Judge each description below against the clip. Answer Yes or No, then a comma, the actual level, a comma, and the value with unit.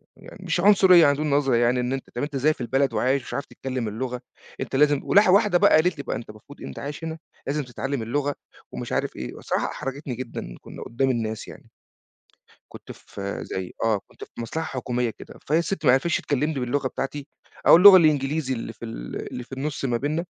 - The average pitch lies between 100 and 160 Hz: Yes, low, 135 Hz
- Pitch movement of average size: Yes, average, 3.8 semitones